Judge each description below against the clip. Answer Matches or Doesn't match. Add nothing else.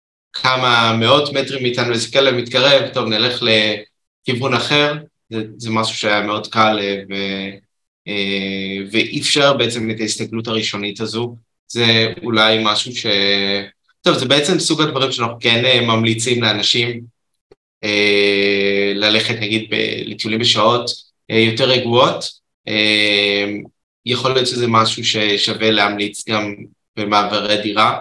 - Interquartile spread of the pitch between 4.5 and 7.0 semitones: Doesn't match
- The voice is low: Matches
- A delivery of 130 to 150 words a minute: Doesn't match